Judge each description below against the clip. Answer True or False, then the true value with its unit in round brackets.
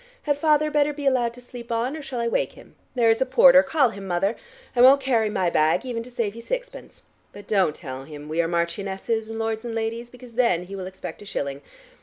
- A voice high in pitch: True (230 Hz)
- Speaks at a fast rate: True (240 wpm)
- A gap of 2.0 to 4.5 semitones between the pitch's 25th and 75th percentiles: False (5.0 semitones)